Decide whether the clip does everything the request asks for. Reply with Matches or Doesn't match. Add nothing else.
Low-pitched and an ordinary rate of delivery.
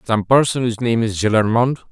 Matches